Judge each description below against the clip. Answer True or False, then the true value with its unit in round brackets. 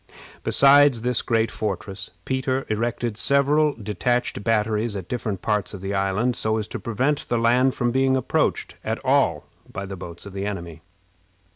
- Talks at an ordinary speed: True (165 wpm)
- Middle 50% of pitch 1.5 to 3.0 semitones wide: False (4.1 semitones)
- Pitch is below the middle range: True (115 Hz)